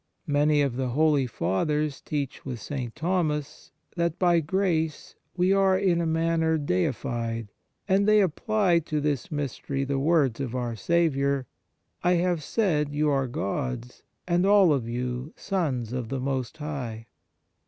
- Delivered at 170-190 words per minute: No, average, 155 wpm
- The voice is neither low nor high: Yes, medium, 150 Hz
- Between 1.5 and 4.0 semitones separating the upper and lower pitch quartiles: No, average, 4.8 semitones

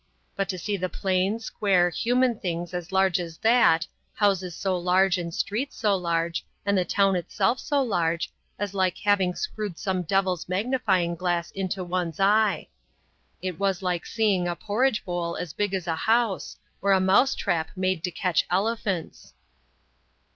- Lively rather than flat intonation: No, narrow, 2.6 semitones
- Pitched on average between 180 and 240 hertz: Yes, high, 190 Hz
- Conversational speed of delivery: Yes, average, 165 wpm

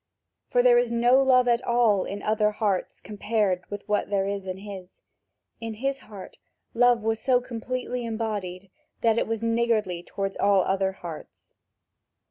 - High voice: Yes, high, 215 Hz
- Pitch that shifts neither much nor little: Yes, average, 3.2 semitones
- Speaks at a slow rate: No, average, 160 wpm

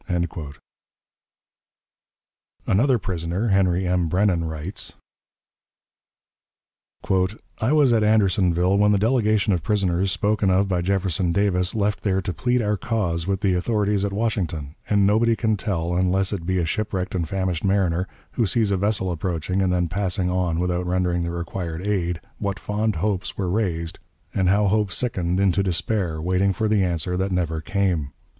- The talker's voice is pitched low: Yes, very low, 95 Hz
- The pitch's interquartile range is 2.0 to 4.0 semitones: Yes, average, 2.8 semitones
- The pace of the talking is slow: No, average, 160 wpm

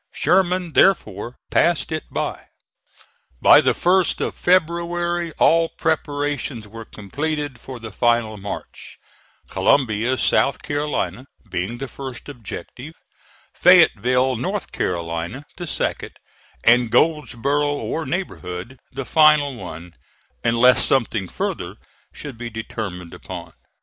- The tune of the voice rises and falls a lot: Yes, wide, 5.7 semitones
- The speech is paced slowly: Yes, slow, 110 wpm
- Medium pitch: No, low, 130 Hz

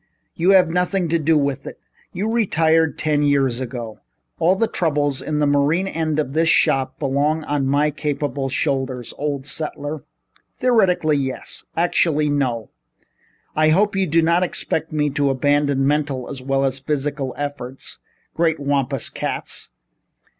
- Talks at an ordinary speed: Yes, average, 150 wpm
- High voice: No, medium, 145 Hz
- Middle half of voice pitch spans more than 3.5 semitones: No, average, 2.9 semitones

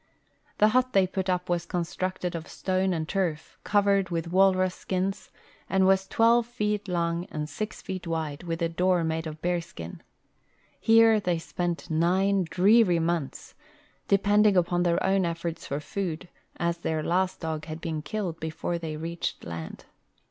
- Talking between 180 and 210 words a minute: No, average, 165 wpm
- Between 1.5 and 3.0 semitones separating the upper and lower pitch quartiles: Yes, average, 2.7 semitones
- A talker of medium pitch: Yes, medium, 175 Hz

